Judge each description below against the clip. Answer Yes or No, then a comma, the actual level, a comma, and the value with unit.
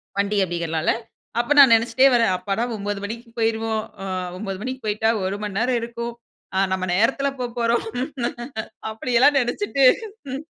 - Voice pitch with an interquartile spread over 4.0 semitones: No, average, 3.1 semitones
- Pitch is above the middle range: Yes, high, 230 Hz